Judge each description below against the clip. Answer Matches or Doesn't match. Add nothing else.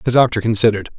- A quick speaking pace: Doesn't match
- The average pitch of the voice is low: Matches